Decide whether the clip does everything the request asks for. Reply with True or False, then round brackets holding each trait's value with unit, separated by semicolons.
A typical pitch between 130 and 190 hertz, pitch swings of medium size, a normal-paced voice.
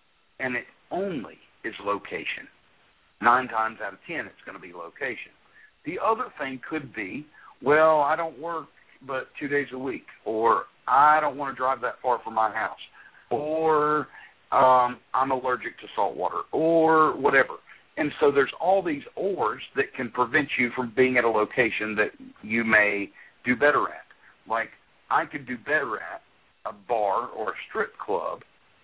True (135 Hz; 4.0 semitones; 170 wpm)